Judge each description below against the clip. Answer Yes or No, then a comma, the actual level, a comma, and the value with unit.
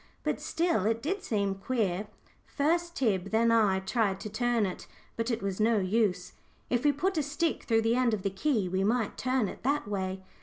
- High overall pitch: Yes, high, 225 Hz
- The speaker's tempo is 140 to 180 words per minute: No, fast, 205 wpm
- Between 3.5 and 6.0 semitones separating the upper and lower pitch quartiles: Yes, average, 4.6 semitones